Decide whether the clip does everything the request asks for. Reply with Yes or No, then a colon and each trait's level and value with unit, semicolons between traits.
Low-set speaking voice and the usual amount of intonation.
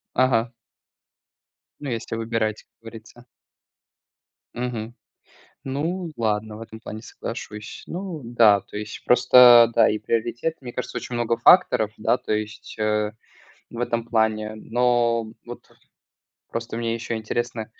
No: low, 115 Hz; narrow, 1.8 semitones